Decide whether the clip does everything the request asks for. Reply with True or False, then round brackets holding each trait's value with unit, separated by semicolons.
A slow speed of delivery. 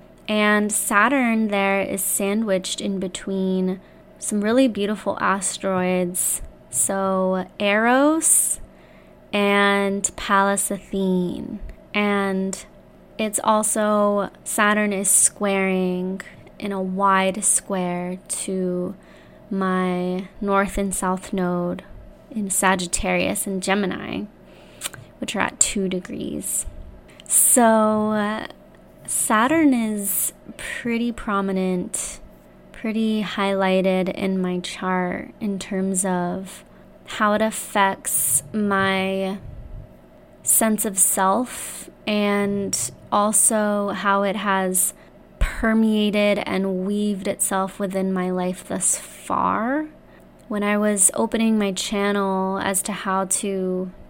True (95 wpm)